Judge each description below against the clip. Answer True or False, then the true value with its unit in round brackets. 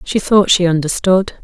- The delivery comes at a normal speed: True (165 wpm)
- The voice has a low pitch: False (185 Hz)